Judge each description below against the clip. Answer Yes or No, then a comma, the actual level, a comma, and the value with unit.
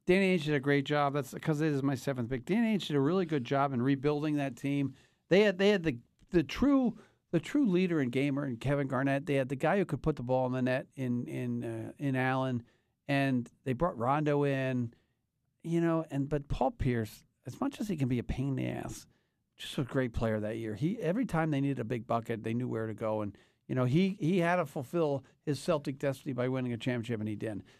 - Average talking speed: No, fast, 250 wpm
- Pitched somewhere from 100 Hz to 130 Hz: No, medium, 140 Hz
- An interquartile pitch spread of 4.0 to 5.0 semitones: Yes, average, 4.3 semitones